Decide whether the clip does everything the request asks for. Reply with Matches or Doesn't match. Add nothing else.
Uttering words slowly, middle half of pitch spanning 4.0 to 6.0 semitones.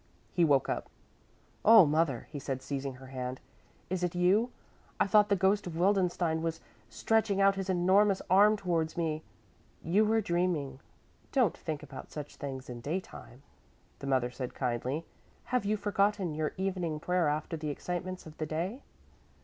Doesn't match